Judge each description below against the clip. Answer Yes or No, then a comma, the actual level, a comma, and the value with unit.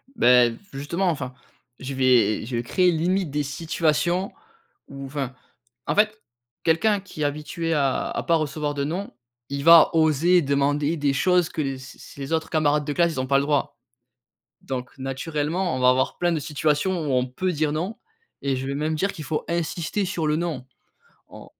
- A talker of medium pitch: Yes, medium, 150 Hz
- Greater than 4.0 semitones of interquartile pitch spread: No, average, 3.6 semitones